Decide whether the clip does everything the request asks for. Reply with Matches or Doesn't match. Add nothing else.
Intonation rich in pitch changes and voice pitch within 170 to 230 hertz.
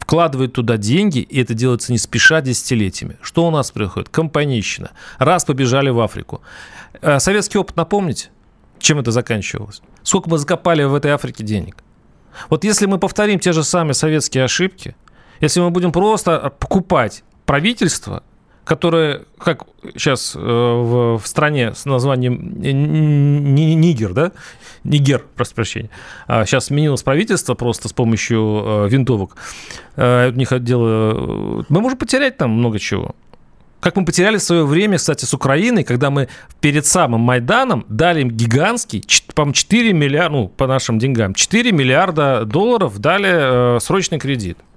Doesn't match